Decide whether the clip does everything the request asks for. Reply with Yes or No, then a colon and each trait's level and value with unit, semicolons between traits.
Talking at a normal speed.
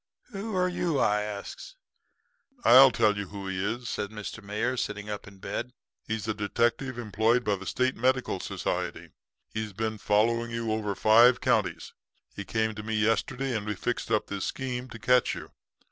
Yes: average, 180 wpm